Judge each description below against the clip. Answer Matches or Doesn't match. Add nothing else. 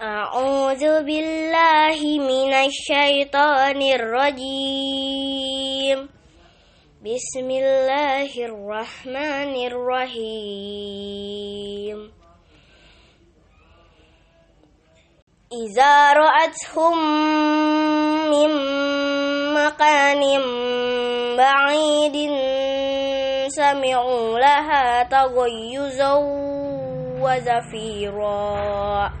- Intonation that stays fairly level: Doesn't match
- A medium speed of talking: Doesn't match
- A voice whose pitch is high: Matches